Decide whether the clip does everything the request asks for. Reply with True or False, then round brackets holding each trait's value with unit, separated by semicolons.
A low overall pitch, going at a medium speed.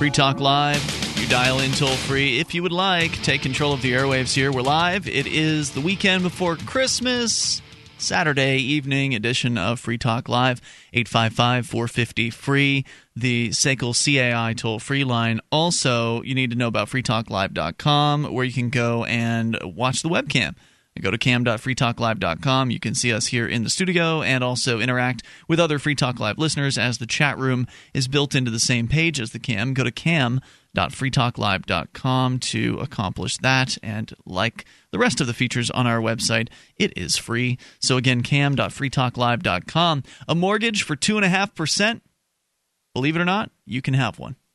True (130 Hz; 170 wpm)